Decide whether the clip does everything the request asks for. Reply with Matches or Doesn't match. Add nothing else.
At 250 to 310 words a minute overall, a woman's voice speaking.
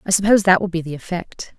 Matches